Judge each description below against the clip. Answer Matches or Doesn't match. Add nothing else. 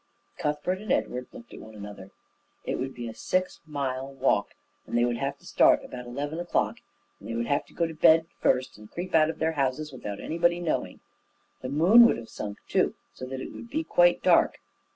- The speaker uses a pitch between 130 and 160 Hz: Matches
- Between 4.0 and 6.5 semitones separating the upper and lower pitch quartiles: Matches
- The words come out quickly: Matches